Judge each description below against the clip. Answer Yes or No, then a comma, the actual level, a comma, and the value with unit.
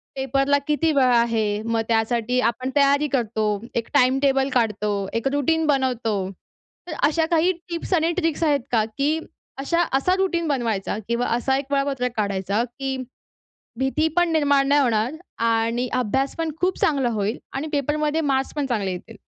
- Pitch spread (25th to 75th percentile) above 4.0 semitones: Yes, average, 4.4 semitones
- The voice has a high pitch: Yes, very high, 265 Hz